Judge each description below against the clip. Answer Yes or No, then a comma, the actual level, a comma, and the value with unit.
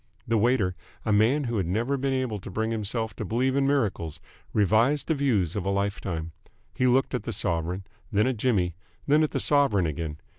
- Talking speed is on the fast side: Yes, fast, 210 wpm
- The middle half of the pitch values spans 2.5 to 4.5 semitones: No, wide, 5.5 semitones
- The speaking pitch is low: Yes, low, 110 Hz